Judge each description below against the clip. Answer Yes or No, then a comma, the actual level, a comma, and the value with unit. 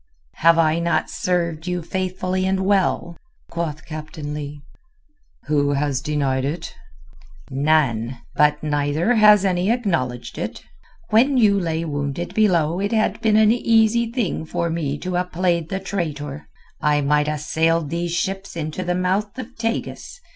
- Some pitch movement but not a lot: Yes, average, 4.4 semitones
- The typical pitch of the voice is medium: Yes, medium, 170 Hz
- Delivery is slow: No, average, 150 wpm